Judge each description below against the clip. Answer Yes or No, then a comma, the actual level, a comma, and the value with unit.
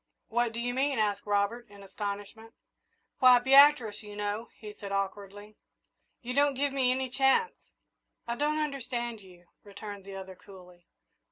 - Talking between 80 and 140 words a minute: No, average, 155 wpm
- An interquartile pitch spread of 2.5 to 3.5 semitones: No, average, 4.2 semitones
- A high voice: Yes, high, 220 Hz